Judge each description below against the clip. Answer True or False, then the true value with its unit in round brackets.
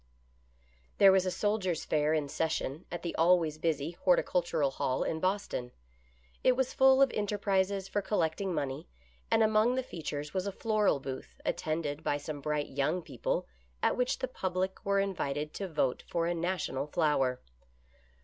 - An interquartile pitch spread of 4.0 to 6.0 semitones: True (4.8 semitones)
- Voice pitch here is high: False (170 Hz)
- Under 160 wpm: False (165 wpm)